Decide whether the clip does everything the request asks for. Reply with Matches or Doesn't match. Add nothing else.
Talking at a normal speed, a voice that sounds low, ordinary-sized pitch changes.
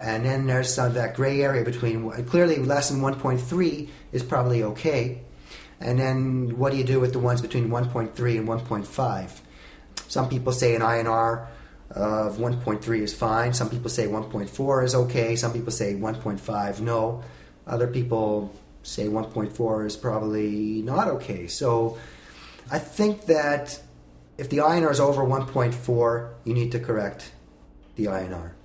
Matches